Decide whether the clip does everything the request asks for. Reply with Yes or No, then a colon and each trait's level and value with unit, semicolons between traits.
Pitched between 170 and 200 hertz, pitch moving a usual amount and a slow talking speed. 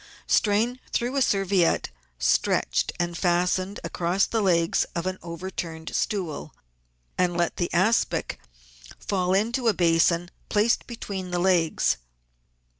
Yes: medium, 185 Hz; average, 3.0 semitones; slow, 120 wpm